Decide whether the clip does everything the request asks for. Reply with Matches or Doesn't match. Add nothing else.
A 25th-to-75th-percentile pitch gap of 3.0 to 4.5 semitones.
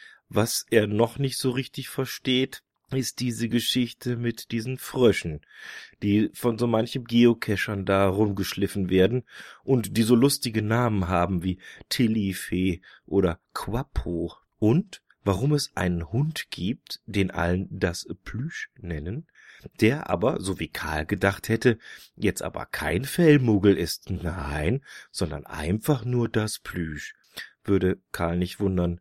Doesn't match